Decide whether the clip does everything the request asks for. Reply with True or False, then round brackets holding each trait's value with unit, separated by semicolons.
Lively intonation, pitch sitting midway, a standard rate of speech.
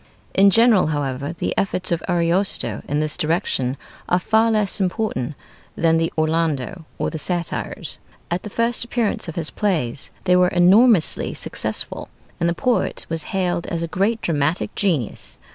False (4.0 semitones; 175 Hz; 160 wpm)